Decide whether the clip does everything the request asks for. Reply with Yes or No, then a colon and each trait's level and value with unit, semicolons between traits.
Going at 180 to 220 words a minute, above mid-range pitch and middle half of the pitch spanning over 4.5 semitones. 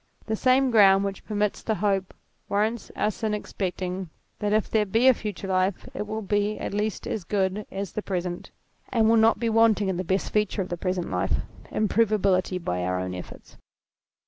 No: average, 200 wpm; high, 205 Hz; narrow, 2.6 semitones